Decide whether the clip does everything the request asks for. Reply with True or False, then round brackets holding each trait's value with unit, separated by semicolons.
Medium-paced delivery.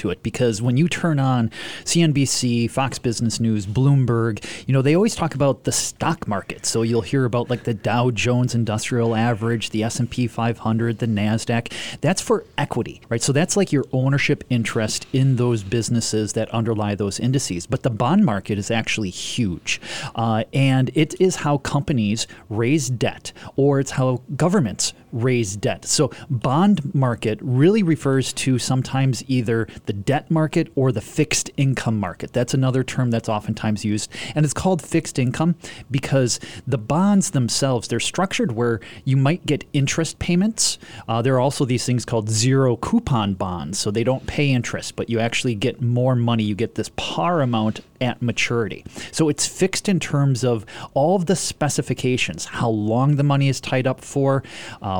True (175 wpm)